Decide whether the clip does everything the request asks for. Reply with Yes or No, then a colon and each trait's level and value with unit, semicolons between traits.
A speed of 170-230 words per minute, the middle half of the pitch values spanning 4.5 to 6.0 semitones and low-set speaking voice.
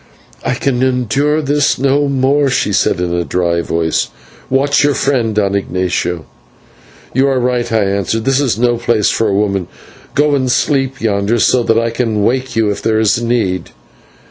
Yes: average, 180 wpm; average, 4.9 semitones; low, 115 Hz